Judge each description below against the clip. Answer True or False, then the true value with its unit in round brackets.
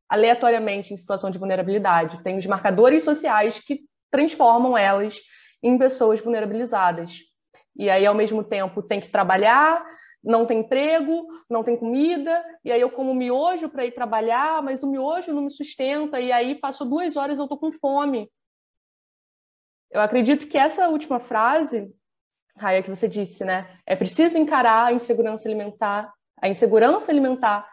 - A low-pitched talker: False (235 Hz)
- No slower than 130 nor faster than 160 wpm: True (155 wpm)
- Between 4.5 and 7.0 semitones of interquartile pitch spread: True (5.5 semitones)